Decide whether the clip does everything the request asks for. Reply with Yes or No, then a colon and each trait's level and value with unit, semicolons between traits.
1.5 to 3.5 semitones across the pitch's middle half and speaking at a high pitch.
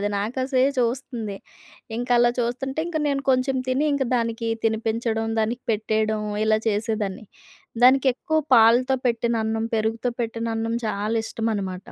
Yes: narrow, 2.4 semitones; high, 230 Hz